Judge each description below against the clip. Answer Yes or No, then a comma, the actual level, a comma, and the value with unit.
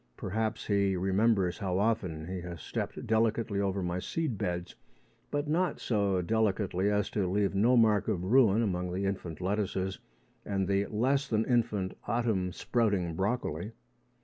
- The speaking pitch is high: No, low, 100 Hz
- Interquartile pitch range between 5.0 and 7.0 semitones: No, average, 3.2 semitones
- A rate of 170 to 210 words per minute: No, average, 150 wpm